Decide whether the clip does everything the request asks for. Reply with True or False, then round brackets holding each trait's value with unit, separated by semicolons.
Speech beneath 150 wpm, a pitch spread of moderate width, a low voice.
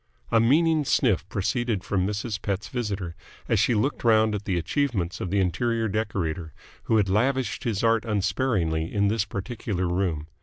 False (165 wpm; 3.7 semitones; 105 Hz)